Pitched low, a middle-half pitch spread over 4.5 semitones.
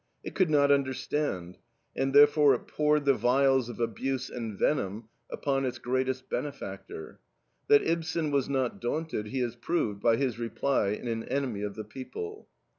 No: low, 130 Hz; average, 3.7 semitones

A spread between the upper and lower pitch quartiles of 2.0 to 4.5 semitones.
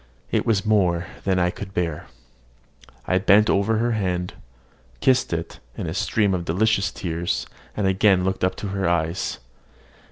Yes: average, 2.8 semitones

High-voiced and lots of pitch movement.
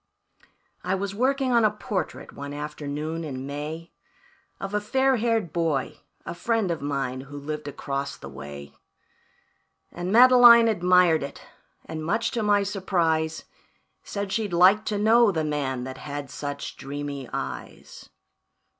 No: medium, 170 Hz; wide, 6.6 semitones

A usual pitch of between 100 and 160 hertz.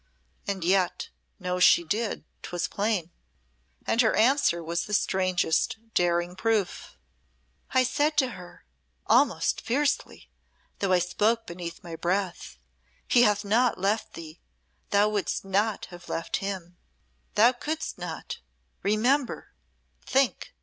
No: high, 200 Hz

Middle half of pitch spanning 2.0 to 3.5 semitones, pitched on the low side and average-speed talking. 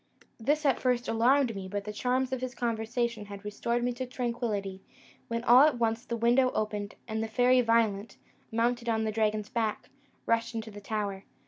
No: narrow, 2.5 semitones; high, 230 Hz; average, 190 wpm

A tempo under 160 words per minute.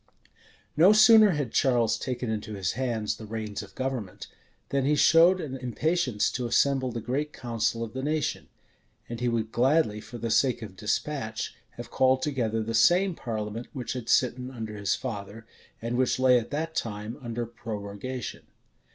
No: average, 175 wpm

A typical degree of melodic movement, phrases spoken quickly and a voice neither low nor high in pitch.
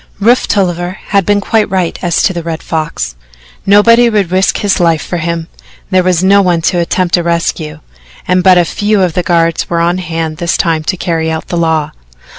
No: narrow, 2.3 semitones; fast, 210 wpm; medium, 175 Hz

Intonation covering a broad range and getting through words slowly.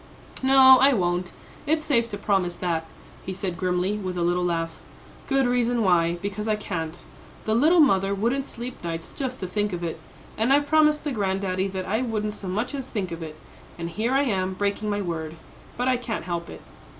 No: wide, 5.7 semitones; fast, 205 wpm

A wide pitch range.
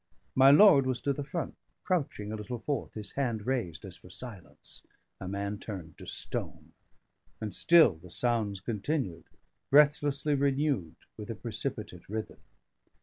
Yes: wide, 5.9 semitones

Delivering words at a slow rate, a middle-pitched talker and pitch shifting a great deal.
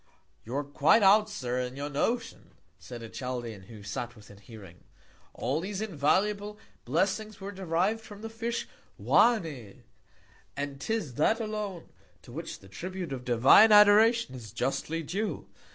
No: average, 150 wpm; medium, 165 Hz; wide, 8.9 semitones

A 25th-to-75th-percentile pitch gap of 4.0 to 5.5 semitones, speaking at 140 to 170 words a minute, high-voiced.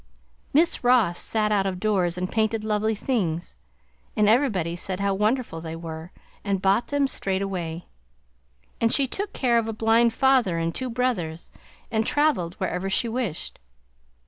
Yes: average, 4.8 semitones; average, 160 wpm; high, 210 Hz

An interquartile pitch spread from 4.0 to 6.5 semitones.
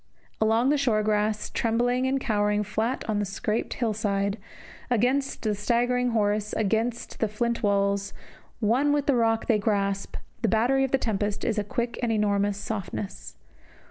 No: average, 2.7 semitones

